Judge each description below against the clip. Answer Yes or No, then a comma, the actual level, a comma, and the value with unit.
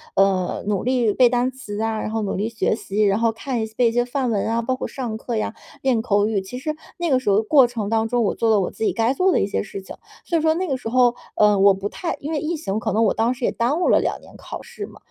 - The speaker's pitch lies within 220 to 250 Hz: Yes, high, 230 Hz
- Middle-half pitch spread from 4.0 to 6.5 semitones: No, average, 3.4 semitones